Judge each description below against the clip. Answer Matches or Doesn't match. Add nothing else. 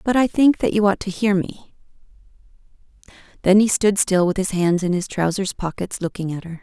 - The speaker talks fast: Matches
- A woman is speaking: Matches